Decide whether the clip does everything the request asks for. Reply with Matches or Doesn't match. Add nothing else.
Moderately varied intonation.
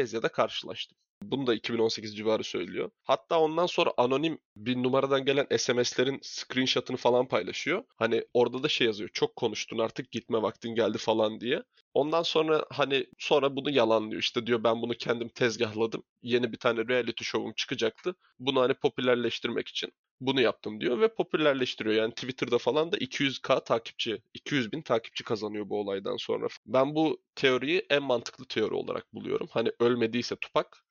Matches